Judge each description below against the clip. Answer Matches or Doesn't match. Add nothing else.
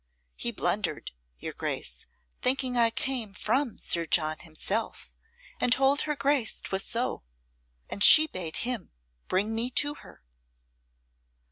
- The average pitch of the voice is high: Matches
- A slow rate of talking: Matches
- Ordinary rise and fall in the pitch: Doesn't match